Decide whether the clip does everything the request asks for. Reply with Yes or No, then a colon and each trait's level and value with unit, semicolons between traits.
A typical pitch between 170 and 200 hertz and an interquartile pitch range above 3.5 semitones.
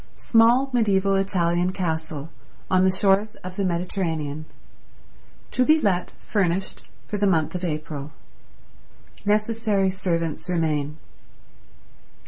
Yes: medium, 185 Hz; average, 3.9 semitones